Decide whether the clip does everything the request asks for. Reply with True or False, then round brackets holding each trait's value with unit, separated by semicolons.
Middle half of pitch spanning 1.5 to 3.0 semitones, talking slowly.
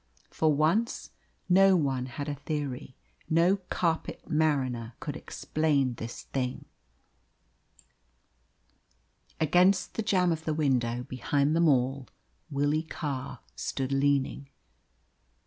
False (3.5 semitones; 105 wpm)